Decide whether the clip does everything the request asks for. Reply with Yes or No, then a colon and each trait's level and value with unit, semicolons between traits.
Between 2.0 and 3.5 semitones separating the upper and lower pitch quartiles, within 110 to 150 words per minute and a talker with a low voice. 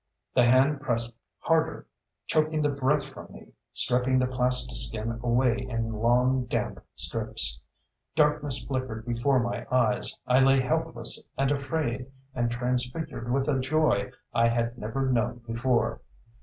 Yes: narrow, 2.6 semitones; slow, 135 wpm; low, 125 Hz